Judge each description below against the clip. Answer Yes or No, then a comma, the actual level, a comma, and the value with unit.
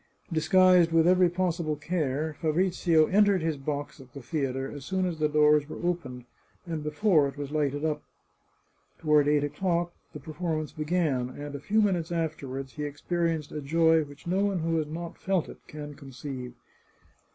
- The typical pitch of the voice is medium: Yes, medium, 155 Hz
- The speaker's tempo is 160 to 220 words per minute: Yes, average, 175 wpm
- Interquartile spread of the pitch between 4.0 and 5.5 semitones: No, average, 3.0 semitones